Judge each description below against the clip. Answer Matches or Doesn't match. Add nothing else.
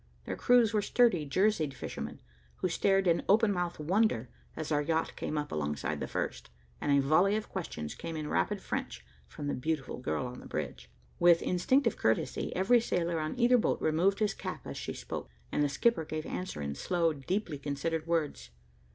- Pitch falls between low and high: Matches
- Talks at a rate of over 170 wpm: Matches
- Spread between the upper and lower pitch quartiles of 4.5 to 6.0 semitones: Matches